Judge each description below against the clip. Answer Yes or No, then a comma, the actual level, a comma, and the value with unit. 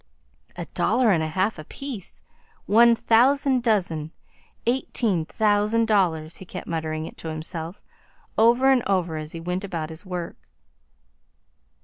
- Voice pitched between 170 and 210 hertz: Yes, high, 190 Hz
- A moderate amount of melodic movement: No, wide, 5.9 semitones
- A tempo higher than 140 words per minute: No, slow, 135 wpm